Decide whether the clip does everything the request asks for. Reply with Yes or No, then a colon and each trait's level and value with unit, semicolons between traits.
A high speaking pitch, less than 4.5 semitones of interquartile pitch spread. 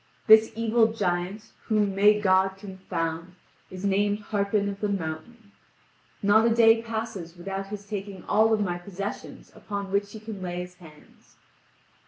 Yes: high, 200 Hz; narrow, 2.5 semitones